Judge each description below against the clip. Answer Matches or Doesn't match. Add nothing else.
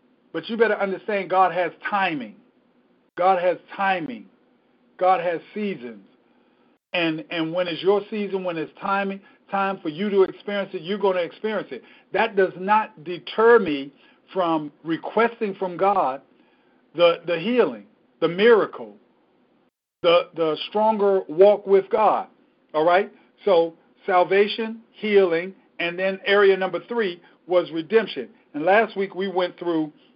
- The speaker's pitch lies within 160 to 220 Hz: Matches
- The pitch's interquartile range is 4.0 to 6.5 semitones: Doesn't match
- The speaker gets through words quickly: Doesn't match